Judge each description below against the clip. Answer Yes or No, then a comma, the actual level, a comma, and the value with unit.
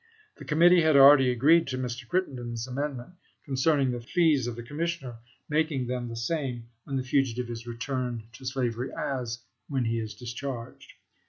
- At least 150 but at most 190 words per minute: Yes, average, 165 wpm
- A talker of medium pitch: No, low, 130 Hz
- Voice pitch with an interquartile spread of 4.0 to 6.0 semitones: No, average, 3.2 semitones